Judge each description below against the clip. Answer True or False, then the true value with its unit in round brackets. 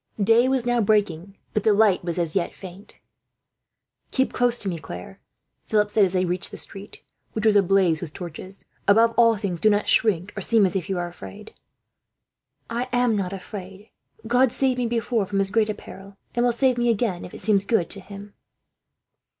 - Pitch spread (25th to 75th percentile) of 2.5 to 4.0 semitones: True (3.7 semitones)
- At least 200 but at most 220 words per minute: True (205 wpm)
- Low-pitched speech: False (205 Hz)